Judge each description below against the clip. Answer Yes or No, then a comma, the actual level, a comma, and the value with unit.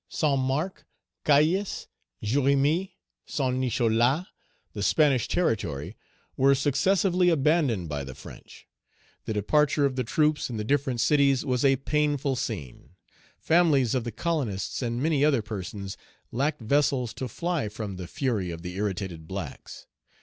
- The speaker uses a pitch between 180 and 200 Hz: No, low, 130 Hz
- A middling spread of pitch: No, wide, 5.8 semitones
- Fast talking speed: No, average, 140 wpm